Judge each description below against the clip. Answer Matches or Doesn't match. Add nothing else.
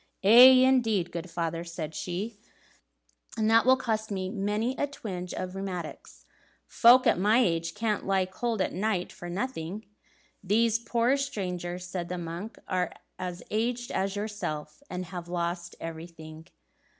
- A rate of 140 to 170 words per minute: Matches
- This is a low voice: Doesn't match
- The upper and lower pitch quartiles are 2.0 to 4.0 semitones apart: Doesn't match